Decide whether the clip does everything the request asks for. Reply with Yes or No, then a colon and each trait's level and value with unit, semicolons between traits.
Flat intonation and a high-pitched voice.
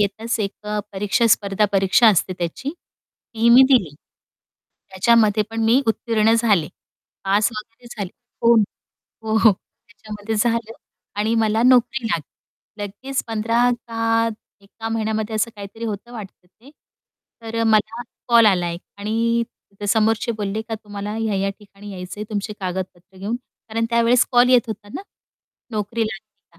Yes: narrow, 2.2 semitones; high, 220 Hz